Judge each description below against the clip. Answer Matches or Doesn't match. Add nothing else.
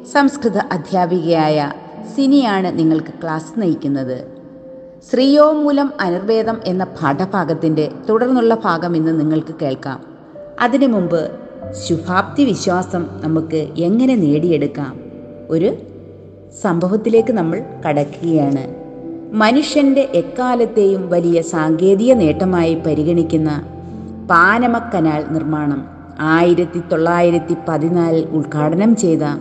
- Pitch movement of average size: Doesn't match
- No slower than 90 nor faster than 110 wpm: Doesn't match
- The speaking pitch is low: Doesn't match